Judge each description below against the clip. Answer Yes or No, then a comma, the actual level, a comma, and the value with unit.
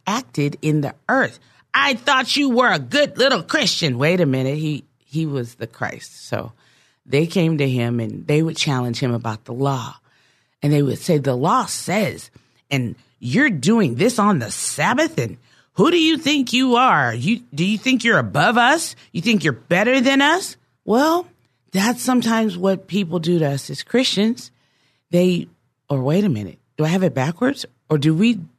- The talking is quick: No, average, 190 wpm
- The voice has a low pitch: No, medium, 175 Hz